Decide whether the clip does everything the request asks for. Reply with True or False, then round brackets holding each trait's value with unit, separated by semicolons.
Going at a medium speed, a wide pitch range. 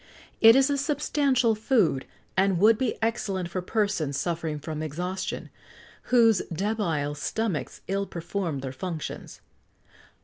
False (125 wpm; 5.7 semitones)